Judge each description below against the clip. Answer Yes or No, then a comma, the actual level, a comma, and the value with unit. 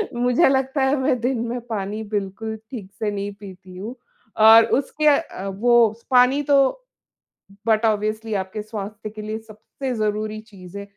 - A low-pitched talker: No, high, 220 Hz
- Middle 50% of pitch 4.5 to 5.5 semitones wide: No, average, 3.2 semitones